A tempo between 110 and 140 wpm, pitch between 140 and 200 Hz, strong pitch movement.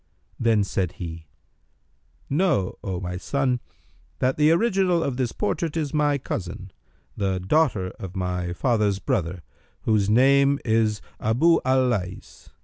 No: slow, 135 wpm; low, 110 Hz; wide, 6.8 semitones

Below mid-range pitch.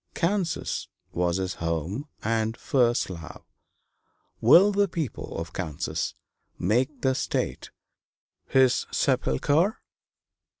Yes: low, 120 Hz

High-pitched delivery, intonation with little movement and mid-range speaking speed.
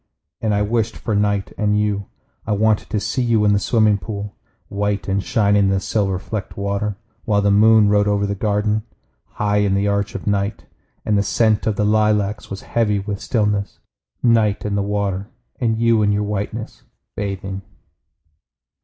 No: low, 105 Hz; narrow, 1.2 semitones; average, 180 wpm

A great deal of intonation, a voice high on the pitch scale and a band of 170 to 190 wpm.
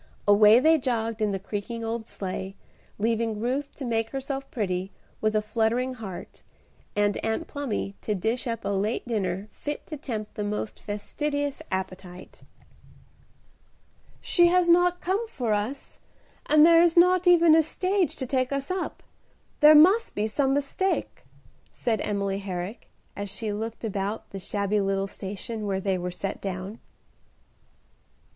No: wide, 6.0 semitones; high, 225 Hz; average, 150 wpm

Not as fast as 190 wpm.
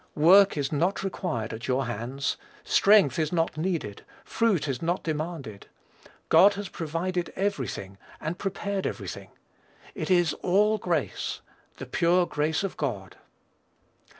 Yes: average, 140 wpm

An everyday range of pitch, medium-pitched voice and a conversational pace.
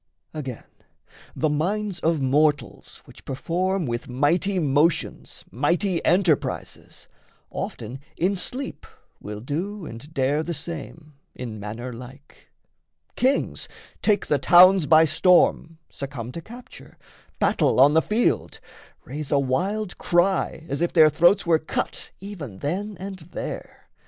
No: average, 5.0 semitones; medium, 160 Hz; slow, 125 wpm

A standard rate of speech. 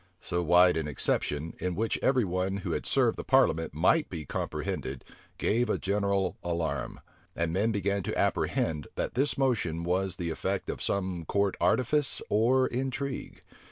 Yes: average, 160 wpm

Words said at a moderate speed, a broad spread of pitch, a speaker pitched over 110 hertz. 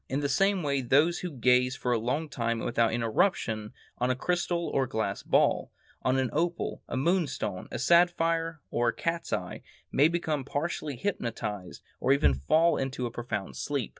Yes: average, 180 wpm; wide, 5.8 semitones; low, 135 Hz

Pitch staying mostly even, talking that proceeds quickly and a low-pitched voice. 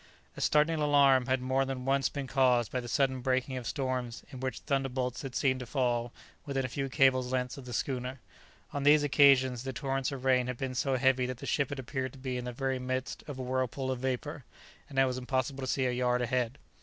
Yes: narrow, 1.2 semitones; fast, 235 wpm; low, 130 Hz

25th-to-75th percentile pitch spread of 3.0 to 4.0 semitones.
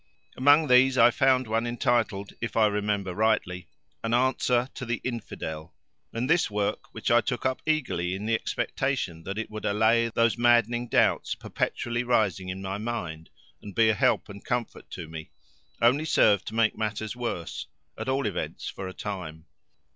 Yes: average, 3.5 semitones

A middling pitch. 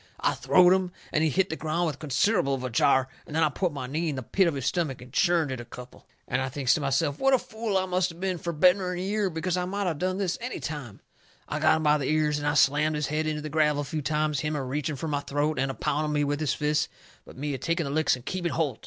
Yes: medium, 155 Hz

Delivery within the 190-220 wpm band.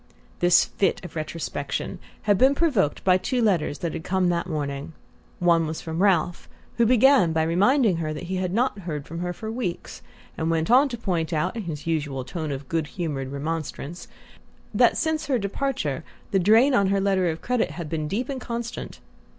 Yes: average, 195 wpm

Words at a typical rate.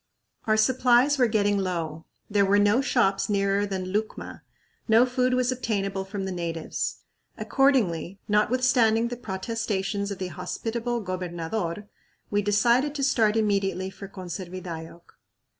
No: slow, 130 wpm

